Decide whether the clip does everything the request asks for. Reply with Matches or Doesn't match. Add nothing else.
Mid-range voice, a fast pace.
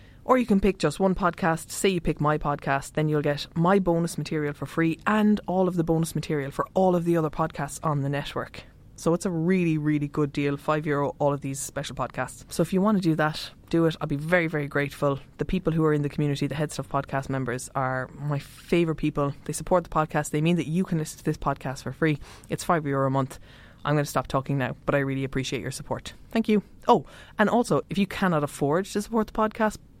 Matches